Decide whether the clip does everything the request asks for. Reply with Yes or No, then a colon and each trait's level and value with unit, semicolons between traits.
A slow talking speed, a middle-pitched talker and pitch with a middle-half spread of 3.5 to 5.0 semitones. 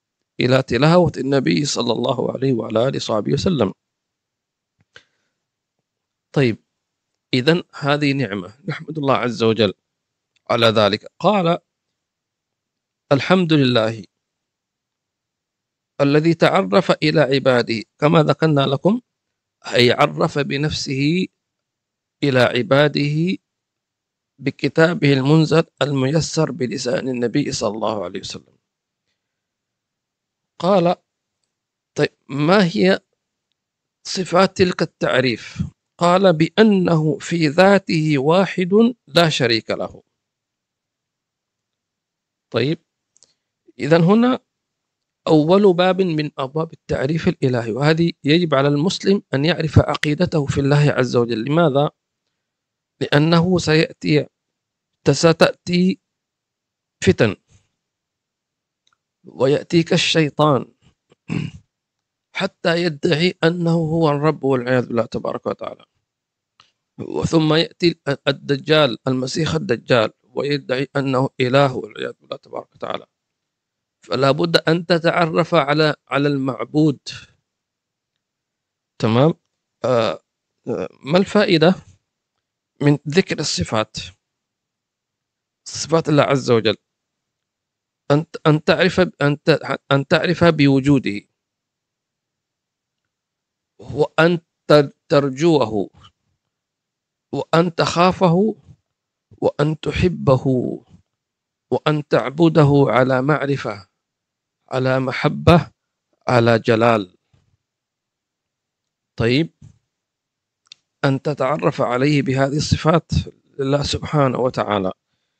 Yes: slow, 80 wpm; medium, 150 Hz; average, 4.2 semitones